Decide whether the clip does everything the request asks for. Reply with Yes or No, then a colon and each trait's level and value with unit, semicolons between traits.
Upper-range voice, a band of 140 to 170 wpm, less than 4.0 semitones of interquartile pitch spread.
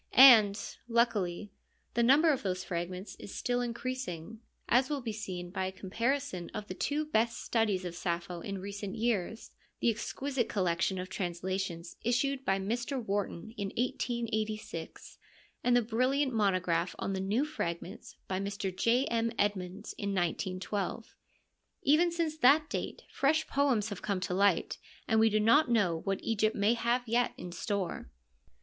No: high, 215 Hz; average, 155 wpm; average, 4.5 semitones